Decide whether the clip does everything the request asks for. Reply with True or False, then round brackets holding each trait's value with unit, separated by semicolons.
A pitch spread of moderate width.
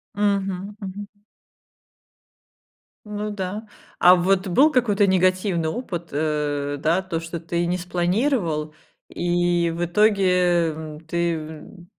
True (3.1 semitones)